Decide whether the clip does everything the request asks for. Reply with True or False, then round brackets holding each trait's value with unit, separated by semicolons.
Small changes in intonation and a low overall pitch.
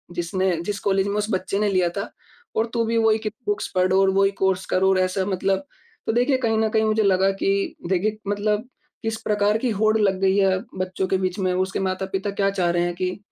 False (2.3 semitones; 195 Hz)